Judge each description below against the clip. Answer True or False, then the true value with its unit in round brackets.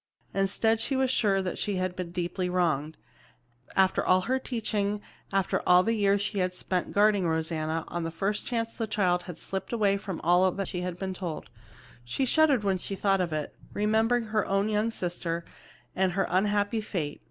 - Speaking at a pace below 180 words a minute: False (190 wpm)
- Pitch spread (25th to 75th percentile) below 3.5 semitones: True (3.0 semitones)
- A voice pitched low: False (195 Hz)